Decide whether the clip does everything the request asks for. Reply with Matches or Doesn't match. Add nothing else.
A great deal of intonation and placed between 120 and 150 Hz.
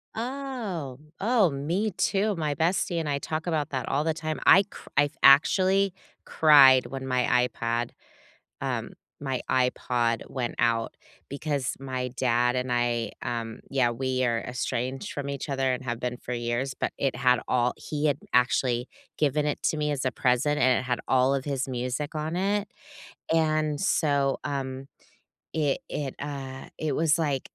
Doesn't match